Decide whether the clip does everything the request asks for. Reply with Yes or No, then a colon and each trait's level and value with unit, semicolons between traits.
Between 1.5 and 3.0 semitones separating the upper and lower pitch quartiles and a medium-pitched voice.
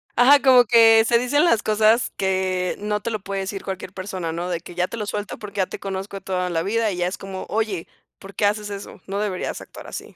No: average, 2.7 semitones; high, 200 Hz